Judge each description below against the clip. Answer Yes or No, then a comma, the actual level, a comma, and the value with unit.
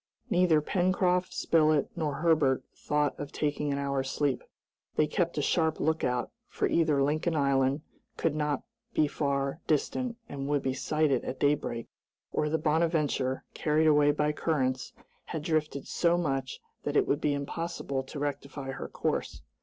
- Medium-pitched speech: Yes, medium, 150 Hz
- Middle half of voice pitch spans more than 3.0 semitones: No, narrow, 2.4 semitones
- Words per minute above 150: Yes, average, 160 wpm